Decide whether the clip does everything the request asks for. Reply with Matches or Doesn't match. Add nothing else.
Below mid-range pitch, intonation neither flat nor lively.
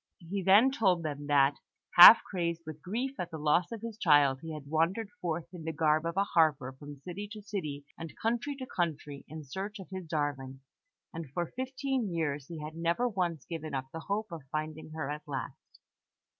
Doesn't match